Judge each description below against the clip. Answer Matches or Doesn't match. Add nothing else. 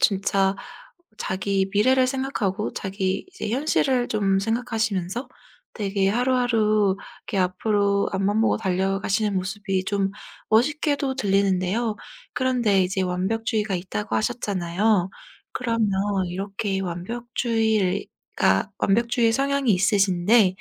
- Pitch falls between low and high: Doesn't match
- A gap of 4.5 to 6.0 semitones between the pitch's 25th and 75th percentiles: Doesn't match